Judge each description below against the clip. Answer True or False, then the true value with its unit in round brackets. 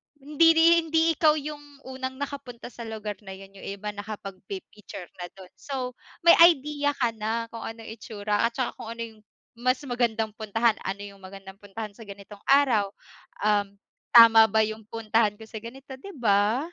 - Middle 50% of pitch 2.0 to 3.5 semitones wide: False (4.1 semitones)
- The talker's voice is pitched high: True (225 Hz)